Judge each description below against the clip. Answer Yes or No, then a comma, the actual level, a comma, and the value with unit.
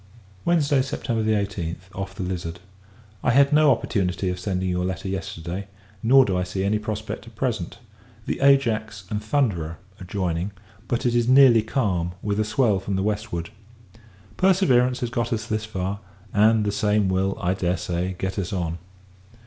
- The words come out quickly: No, average, 175 wpm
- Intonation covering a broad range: No, average, 4.1 semitones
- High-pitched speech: No, low, 105 Hz